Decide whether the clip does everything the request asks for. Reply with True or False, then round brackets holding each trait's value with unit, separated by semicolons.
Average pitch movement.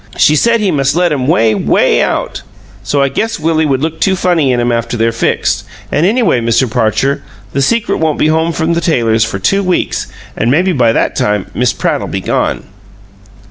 False (6.3 semitones)